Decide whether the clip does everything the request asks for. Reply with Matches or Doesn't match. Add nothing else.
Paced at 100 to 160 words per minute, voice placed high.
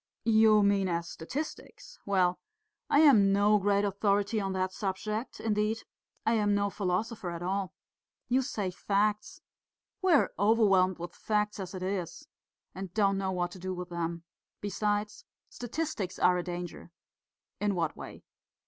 Matches